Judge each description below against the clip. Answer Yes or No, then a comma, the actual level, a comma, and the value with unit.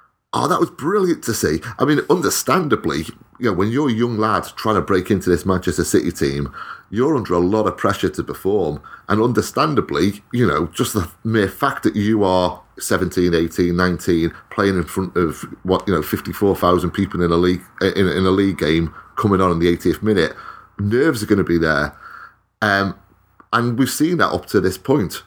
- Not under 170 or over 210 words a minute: Yes, average, 200 wpm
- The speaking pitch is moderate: No, very low, 95 Hz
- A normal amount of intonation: Yes, average, 3.1 semitones